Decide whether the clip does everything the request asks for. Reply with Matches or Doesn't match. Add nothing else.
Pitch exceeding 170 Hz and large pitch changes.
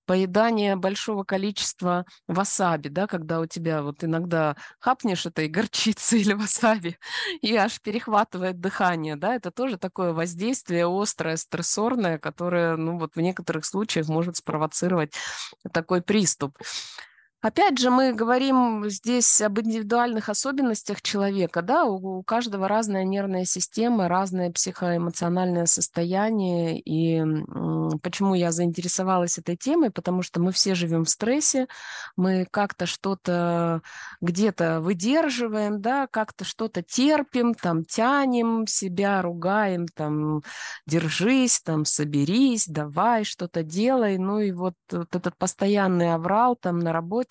Doesn't match